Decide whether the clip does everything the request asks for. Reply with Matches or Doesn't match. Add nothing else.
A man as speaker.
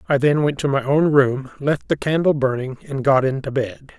Matches